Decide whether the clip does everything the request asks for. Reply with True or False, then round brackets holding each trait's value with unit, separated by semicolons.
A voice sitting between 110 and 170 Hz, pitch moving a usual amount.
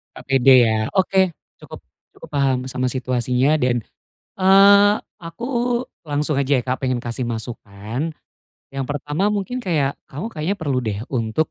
False (140 Hz; 6.8 semitones)